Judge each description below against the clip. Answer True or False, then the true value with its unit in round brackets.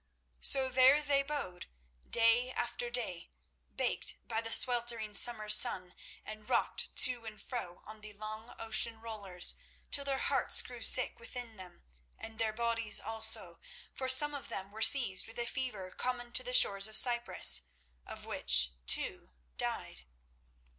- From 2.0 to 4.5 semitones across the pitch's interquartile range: True (2.8 semitones)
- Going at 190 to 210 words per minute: False (155 wpm)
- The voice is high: True (230 Hz)